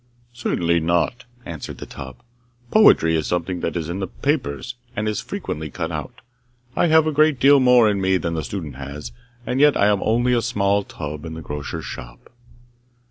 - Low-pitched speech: Yes, very low, 95 Hz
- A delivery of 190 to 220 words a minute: Yes, average, 195 wpm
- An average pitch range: No, wide, 7.4 semitones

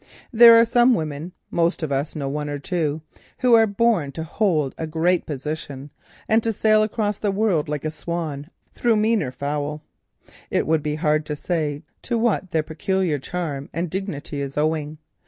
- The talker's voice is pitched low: No, medium, 160 Hz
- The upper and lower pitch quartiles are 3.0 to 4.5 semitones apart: No, average, 5.3 semitones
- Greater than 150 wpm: Yes, average, 175 wpm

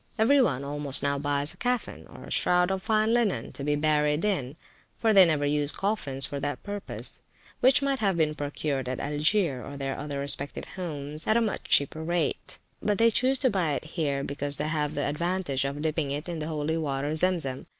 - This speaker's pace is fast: Yes, fast, 210 wpm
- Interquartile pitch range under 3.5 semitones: No, average, 4.9 semitones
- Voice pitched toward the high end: No, medium, 150 Hz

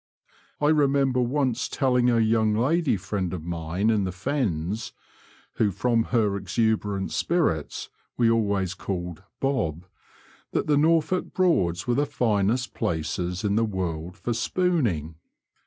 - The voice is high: No, low, 110 Hz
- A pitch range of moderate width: No, wide, 6.0 semitones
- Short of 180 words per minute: Yes, average, 140 wpm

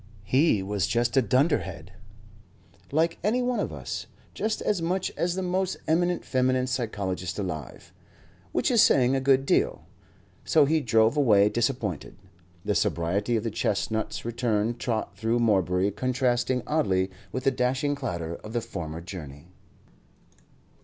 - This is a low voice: Yes, low, 120 Hz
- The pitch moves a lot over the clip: Yes, wide, 5.8 semitones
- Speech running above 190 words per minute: No, average, 145 wpm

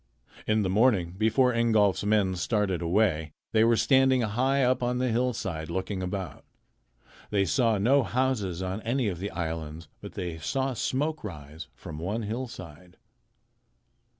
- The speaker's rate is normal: Yes, average, 150 wpm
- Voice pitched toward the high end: No, low, 105 Hz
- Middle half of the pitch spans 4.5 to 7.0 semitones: Yes, wide, 5.4 semitones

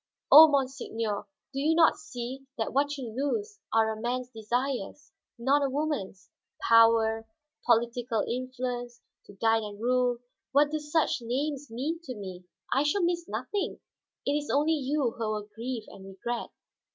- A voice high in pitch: Yes, very high, 250 Hz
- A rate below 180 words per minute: Yes, average, 155 wpm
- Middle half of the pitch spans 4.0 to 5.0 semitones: Yes, average, 4.4 semitones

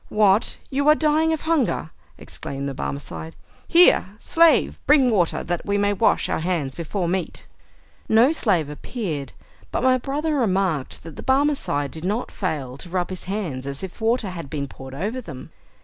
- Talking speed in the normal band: Yes, average, 180 wpm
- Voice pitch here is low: No, high, 190 Hz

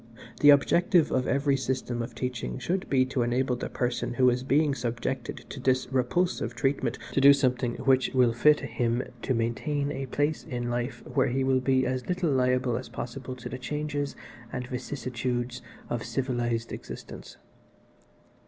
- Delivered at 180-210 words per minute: No, average, 165 wpm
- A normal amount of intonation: No, narrow, 2.2 semitones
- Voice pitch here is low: Yes, low, 130 Hz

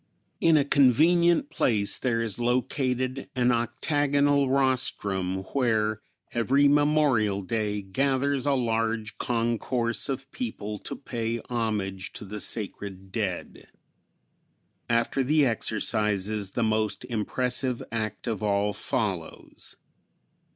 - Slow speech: Yes, slow, 110 wpm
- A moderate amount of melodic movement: Yes, average, 4.1 semitones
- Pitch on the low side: Yes, low, 115 Hz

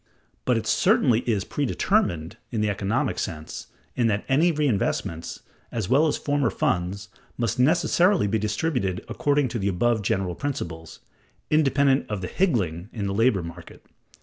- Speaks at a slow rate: No, average, 150 wpm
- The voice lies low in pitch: Yes, low, 110 Hz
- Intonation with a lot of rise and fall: Yes, wide, 6.8 semitones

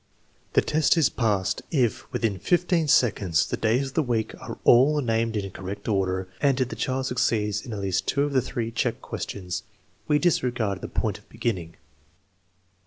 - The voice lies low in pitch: Yes, low, 115 Hz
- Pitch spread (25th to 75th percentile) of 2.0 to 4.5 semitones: No, average, 5.0 semitones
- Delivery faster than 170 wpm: Yes, average, 180 wpm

